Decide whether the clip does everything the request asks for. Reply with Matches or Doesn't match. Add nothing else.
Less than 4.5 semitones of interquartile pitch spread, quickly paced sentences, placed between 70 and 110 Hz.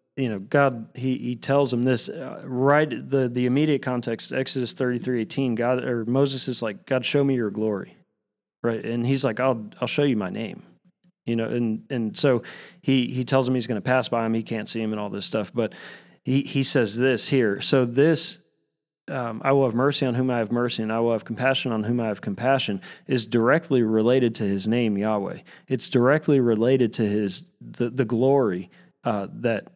Doesn't match